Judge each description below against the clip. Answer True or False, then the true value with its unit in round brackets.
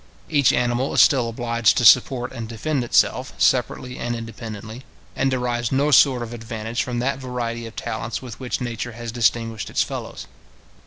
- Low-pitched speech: True (120 Hz)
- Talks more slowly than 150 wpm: False (170 wpm)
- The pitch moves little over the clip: True (1.8 semitones)